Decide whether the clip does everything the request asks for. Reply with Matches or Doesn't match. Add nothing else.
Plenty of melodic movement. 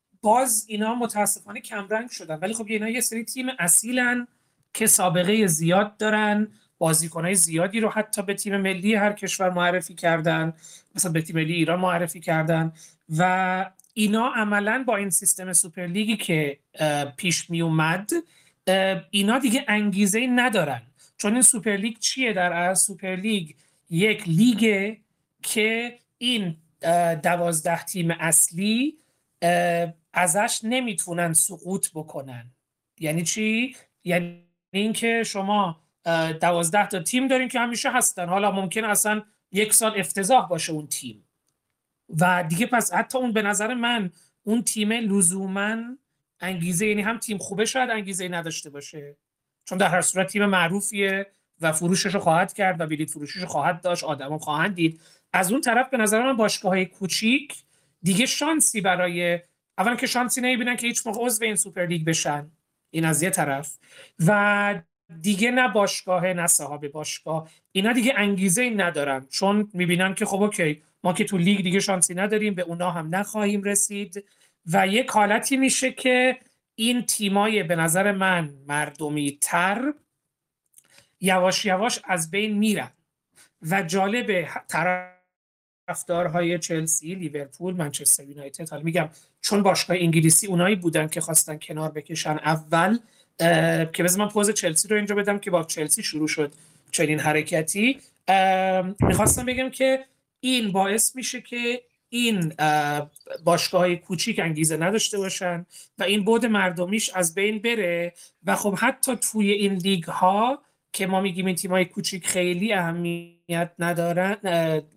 Doesn't match